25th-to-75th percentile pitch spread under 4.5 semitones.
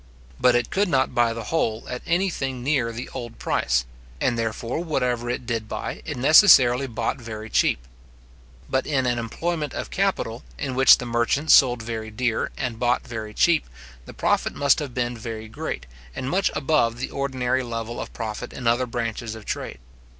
Yes: narrow, 2.6 semitones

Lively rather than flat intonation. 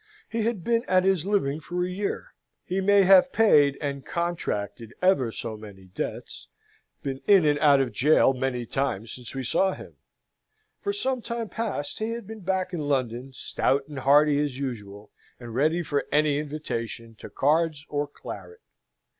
Yes: wide, 6.3 semitones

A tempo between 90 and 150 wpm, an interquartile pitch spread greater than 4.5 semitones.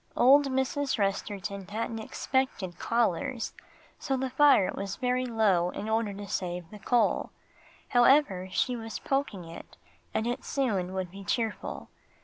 Yes: average, 140 wpm; average, 4.9 semitones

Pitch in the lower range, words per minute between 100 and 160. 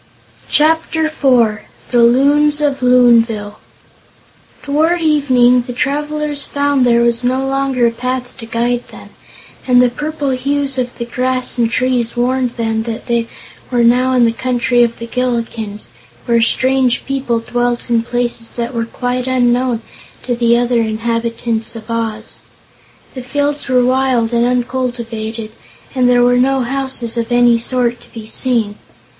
No: high, 245 Hz; average, 150 wpm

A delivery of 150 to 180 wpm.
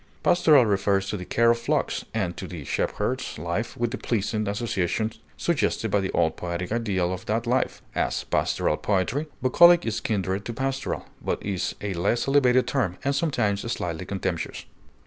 Yes: average, 170 wpm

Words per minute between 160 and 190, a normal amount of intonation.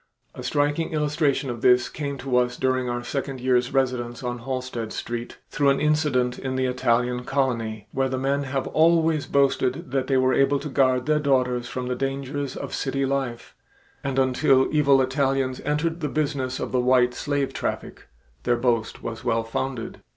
No: average, 180 wpm; narrow, 2.0 semitones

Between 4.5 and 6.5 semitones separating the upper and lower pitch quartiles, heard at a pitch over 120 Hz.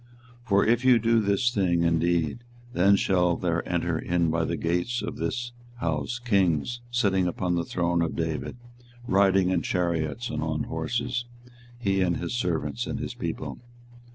No: average, 5.0 semitones; very low, 90 Hz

